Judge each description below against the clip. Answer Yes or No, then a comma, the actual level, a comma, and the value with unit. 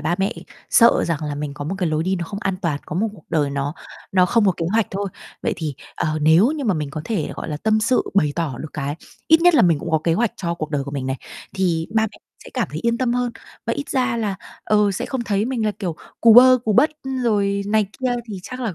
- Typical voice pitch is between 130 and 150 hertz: No, high, 195 Hz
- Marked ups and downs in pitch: Yes, wide, 6.3 semitones